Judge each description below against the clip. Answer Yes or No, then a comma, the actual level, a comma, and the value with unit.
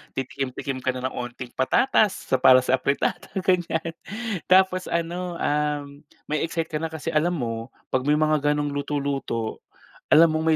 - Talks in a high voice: No, medium, 150 Hz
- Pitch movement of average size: Yes, average, 4.0 semitones